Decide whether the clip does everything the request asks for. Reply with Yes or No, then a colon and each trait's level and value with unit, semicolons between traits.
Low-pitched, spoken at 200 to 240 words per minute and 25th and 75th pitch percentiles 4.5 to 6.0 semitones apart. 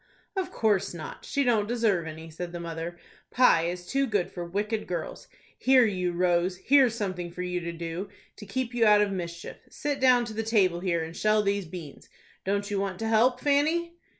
No: high, 200 Hz; fast, 205 wpm; average, 5.0 semitones